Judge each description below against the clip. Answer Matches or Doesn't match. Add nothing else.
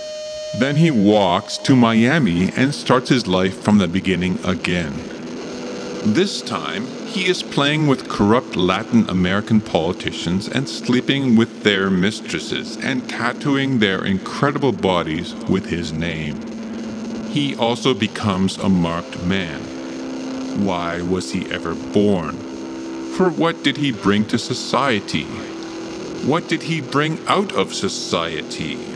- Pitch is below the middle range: Matches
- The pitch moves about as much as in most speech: Doesn't match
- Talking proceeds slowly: Matches